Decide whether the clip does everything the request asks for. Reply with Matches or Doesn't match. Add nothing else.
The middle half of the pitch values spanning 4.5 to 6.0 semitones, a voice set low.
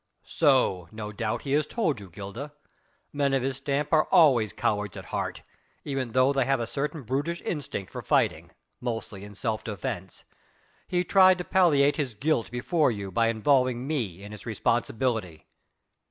Matches